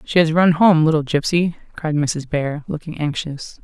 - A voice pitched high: No, medium, 155 Hz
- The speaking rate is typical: Yes, average, 180 wpm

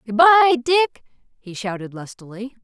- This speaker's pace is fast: No, slow, 135 wpm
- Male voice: No, female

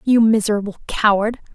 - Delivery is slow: Yes, slow, 115 wpm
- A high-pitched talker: Yes, high, 215 Hz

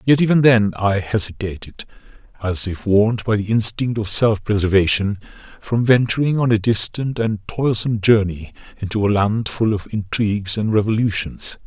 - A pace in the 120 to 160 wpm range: Yes, average, 155 wpm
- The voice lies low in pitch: Yes, low, 105 Hz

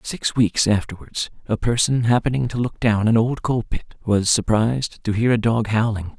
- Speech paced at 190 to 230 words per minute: Yes, average, 195 wpm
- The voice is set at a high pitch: No, low, 110 Hz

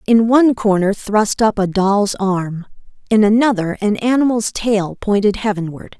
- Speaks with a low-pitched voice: No, high, 210 Hz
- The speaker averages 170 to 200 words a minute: No, average, 150 wpm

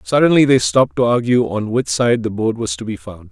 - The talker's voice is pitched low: Yes, low, 120 Hz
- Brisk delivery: Yes, fast, 255 wpm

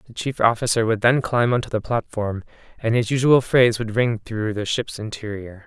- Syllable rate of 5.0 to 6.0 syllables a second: Yes, 5.2 syllables/s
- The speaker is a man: Yes, male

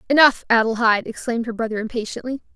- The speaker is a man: No, female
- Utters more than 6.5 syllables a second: Yes, 7.2 syllables/s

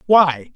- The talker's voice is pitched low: No, medium, 160 Hz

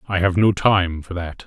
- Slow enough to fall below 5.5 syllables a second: Yes, 4.7 syllables/s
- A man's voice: Yes, male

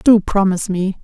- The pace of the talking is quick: No, average, 175 wpm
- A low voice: No, high, 195 Hz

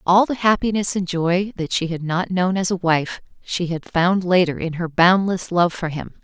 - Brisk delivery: Yes, fast, 220 wpm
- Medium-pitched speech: Yes, medium, 180 Hz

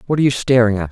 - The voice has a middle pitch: No, low, 120 Hz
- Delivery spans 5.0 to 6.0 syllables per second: No, 8.8 syllables/s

